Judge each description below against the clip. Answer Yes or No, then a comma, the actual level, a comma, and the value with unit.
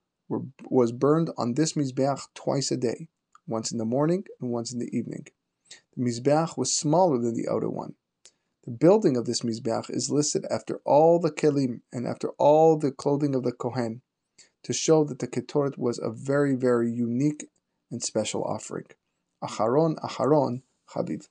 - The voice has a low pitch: Yes, low, 130 Hz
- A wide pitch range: No, average, 3.8 semitones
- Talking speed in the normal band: Yes, average, 170 wpm